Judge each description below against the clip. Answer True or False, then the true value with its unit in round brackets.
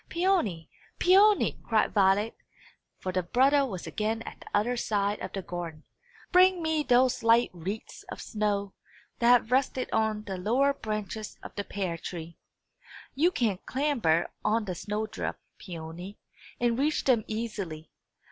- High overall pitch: True (215 Hz)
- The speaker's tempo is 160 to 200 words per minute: False (150 wpm)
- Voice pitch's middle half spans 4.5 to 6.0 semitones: True (4.8 semitones)